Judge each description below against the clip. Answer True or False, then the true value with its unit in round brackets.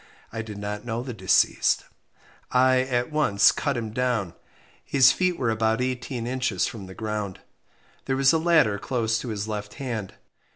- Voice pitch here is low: True (115 Hz)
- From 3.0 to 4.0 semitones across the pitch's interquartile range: True (3.4 semitones)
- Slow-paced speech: False (170 wpm)